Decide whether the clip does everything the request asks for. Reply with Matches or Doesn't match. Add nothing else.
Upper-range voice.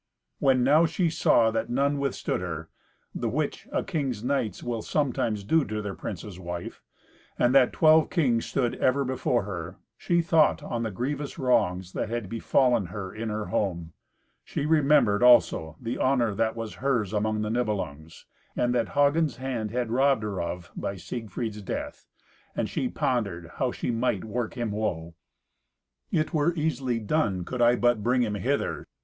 Doesn't match